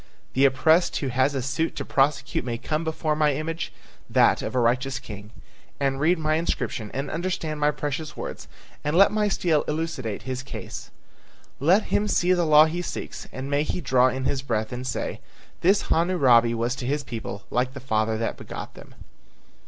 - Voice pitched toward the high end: No, medium, 140 Hz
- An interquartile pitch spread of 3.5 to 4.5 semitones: Yes, average, 3.9 semitones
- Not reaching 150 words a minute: No, average, 190 wpm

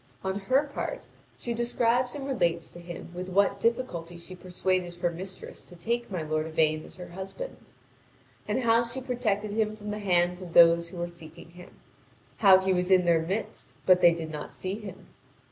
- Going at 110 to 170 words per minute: No, average, 195 wpm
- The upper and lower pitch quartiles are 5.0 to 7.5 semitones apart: No, average, 4.4 semitones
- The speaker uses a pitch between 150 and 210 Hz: Yes, medium, 185 Hz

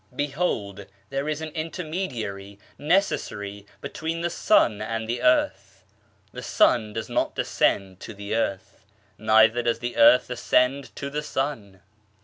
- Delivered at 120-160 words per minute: Yes, slow, 135 wpm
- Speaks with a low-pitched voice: Yes, low, 120 Hz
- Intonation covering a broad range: Yes, wide, 6.3 semitones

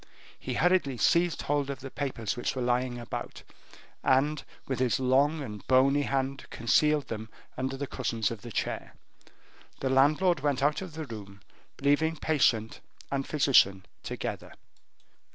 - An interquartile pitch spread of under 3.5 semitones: Yes, average, 3.1 semitones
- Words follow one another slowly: No, average, 150 wpm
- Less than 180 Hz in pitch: Yes, low, 135 Hz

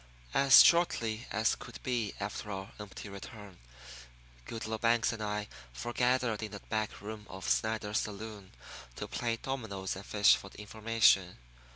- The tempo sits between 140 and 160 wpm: Yes, average, 145 wpm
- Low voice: Yes, low, 110 Hz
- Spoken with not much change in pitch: Yes, narrow, 2.1 semitones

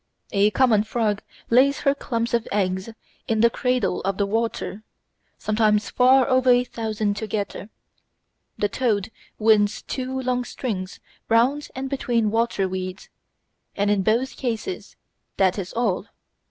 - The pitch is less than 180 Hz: No, high, 225 Hz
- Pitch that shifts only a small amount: No, average, 3.4 semitones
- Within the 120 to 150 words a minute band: Yes, average, 140 wpm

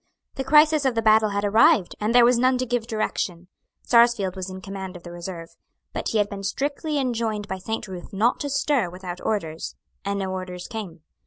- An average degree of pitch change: Yes, average, 4.3 semitones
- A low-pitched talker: No, high, 210 Hz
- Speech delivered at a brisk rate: Yes, fast, 210 wpm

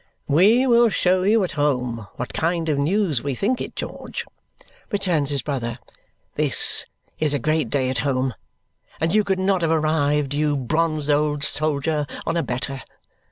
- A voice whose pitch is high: No, medium, 150 Hz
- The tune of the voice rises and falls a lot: No, average, 3.9 semitones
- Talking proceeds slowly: No, average, 165 wpm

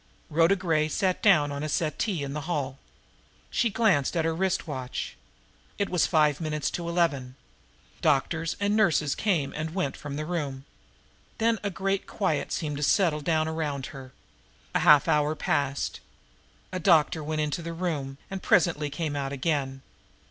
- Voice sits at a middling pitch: Yes, medium, 155 Hz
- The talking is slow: No, average, 165 wpm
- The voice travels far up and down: No, average, 3.5 semitones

